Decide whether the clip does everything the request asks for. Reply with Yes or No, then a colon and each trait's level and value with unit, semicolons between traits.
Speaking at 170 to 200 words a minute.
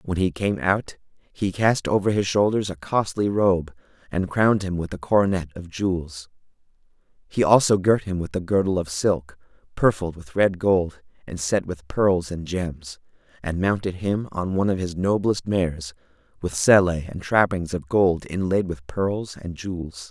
Yes: average, 175 wpm